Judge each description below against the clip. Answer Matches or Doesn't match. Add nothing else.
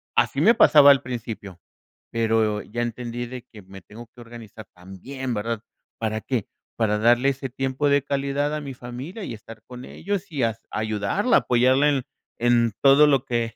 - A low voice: Matches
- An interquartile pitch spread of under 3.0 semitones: Doesn't match